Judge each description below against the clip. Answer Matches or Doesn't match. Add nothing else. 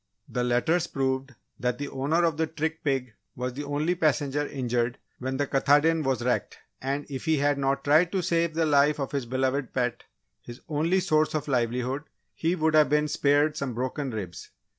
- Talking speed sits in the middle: Matches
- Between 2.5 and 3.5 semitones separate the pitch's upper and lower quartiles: Matches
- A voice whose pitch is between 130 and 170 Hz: Matches